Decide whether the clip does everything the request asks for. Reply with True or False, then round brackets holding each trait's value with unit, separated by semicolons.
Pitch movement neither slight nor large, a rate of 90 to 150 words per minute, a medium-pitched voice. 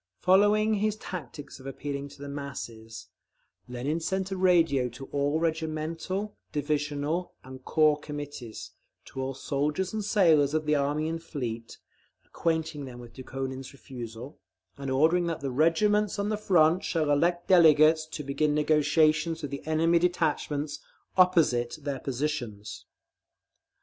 True (3.3 semitones; 140 wpm; 150 Hz)